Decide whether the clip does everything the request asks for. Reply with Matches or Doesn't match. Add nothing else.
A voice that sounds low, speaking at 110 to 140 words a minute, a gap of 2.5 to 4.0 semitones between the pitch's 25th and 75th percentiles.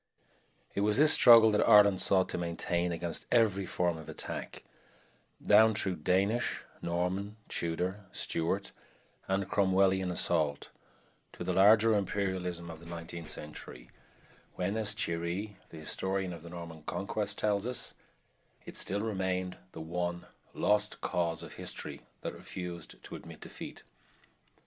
Matches